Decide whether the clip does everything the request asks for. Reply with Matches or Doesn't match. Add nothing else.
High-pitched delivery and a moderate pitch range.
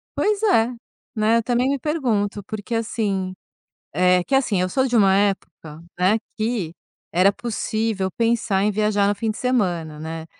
Matches